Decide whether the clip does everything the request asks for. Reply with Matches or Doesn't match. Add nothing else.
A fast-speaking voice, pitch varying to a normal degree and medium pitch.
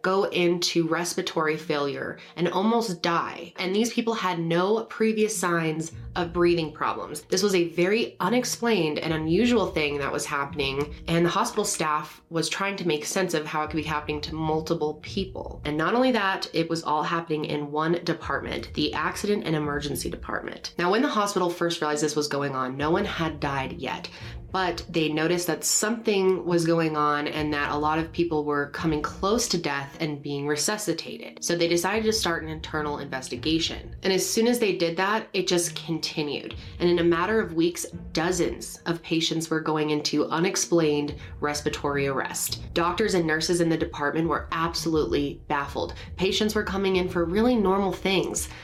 Doesn't match